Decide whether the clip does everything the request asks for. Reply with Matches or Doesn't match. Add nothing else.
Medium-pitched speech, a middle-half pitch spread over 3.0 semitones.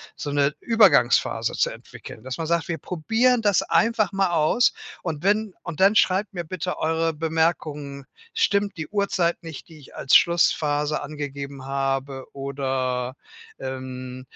Matches